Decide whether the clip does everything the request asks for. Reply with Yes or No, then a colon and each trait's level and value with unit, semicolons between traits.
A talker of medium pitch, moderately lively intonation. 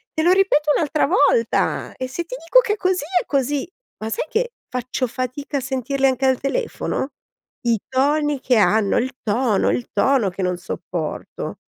No: very high, 265 Hz; average, 4.1 semitones